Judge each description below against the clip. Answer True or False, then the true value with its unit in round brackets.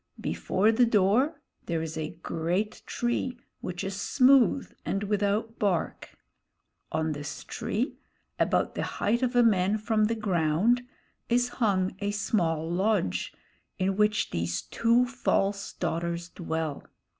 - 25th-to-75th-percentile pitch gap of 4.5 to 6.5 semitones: True (5.2 semitones)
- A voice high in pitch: True (200 Hz)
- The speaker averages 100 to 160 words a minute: True (135 wpm)